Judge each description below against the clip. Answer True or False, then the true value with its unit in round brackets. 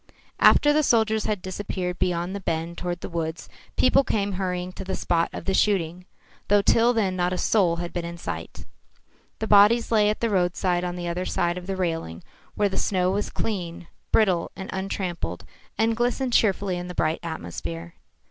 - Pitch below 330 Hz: True (185 Hz)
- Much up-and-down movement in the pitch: False (3.0 semitones)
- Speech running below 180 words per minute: False (190 wpm)